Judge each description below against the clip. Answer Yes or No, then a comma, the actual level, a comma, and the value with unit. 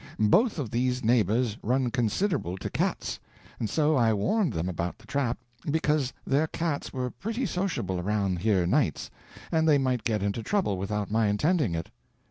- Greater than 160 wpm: Yes, average, 170 wpm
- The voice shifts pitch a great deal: Yes, wide, 6.6 semitones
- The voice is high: No, low, 120 Hz